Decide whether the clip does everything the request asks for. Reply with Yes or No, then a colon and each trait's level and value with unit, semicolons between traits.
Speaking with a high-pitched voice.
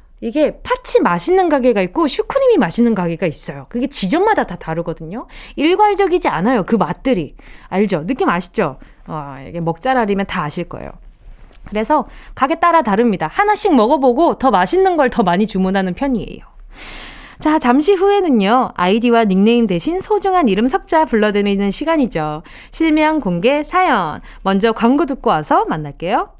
Yes: high, 240 Hz